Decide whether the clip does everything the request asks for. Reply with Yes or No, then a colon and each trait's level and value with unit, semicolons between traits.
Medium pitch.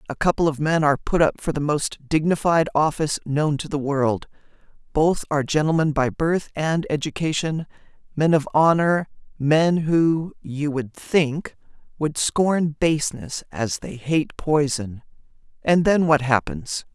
Yes: medium, 155 Hz